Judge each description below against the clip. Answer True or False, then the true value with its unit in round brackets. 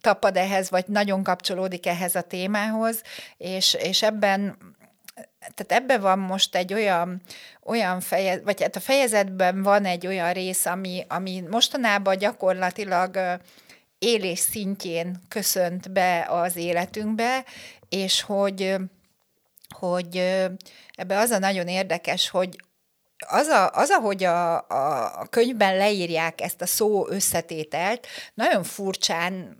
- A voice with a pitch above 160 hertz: True (190 Hz)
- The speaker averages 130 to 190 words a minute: False (120 wpm)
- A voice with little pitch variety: True (2.3 semitones)